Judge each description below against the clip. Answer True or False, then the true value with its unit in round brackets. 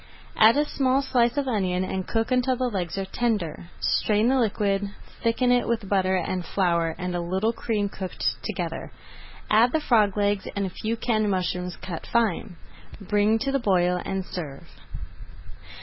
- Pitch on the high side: True (205 Hz)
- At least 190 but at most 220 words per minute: False (170 wpm)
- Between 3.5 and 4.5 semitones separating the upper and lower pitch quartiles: True (4.1 semitones)